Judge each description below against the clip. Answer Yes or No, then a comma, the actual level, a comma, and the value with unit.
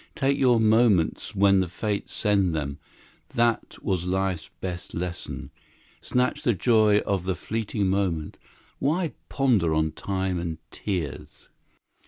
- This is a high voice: No, very low, 95 Hz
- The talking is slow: Yes, slow, 130 wpm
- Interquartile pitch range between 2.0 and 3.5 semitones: No, average, 4.1 semitones